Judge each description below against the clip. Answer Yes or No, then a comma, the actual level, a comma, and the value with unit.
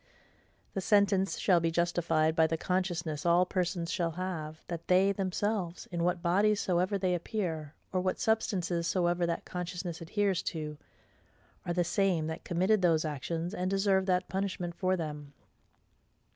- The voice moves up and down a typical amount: No, narrow, 2.2 semitones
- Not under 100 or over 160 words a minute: Yes, average, 155 wpm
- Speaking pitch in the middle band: Yes, medium, 175 Hz